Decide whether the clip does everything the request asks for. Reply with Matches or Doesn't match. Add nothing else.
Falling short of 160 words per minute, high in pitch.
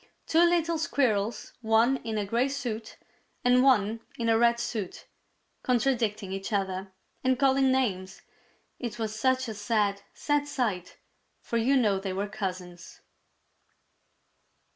Matches